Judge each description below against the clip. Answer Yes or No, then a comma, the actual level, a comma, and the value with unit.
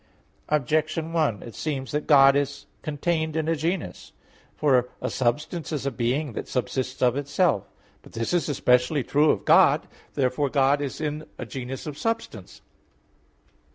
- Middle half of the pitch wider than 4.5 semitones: No, average, 3.3 semitones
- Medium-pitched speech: Yes, medium, 145 Hz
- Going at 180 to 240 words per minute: No, average, 155 wpm